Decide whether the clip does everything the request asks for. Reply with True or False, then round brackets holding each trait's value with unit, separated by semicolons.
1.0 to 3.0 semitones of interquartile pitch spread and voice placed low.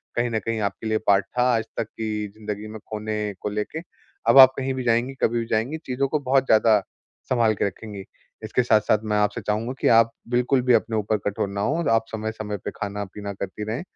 True (2.5 semitones; 110 Hz)